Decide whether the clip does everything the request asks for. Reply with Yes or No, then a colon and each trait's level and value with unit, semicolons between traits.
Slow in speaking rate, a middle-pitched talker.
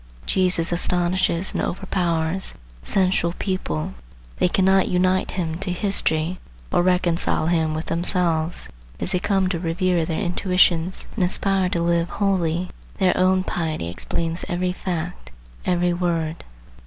Yes: slow, 130 wpm; medium, 180 Hz